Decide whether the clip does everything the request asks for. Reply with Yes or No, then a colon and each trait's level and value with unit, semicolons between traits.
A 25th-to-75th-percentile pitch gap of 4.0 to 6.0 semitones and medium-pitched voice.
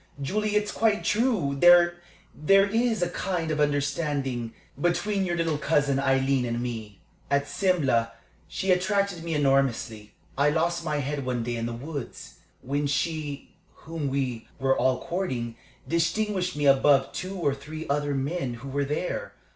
Yes: average, 4.7 semitones; medium, 145 Hz